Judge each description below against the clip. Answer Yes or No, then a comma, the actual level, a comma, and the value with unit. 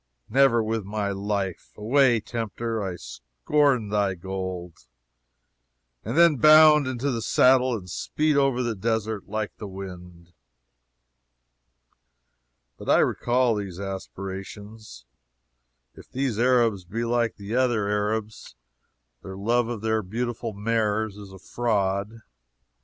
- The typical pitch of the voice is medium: No, low, 110 Hz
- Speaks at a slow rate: Yes, slow, 120 wpm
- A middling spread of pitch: Yes, average, 3.5 semitones